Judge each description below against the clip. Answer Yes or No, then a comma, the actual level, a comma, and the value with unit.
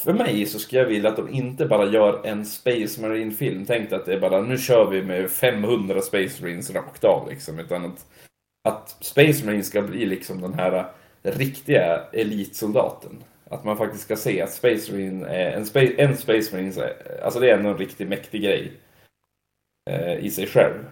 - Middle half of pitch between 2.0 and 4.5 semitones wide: No, average, 5.2 semitones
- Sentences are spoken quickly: No, average, 185 wpm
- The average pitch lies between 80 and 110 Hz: Yes, low, 105 Hz